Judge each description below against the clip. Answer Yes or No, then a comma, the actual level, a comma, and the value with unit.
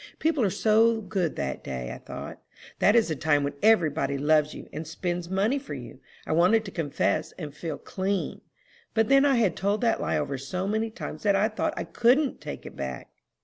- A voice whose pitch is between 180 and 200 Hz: Yes, high, 190 Hz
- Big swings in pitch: Yes, wide, 6.7 semitones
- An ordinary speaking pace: No, fast, 215 wpm